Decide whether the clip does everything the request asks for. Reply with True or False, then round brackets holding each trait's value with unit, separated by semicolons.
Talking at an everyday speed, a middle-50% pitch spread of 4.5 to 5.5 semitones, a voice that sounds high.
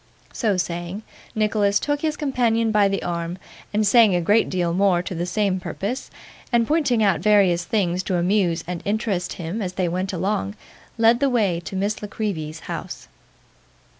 False (175 wpm; 3.7 semitones; 195 Hz)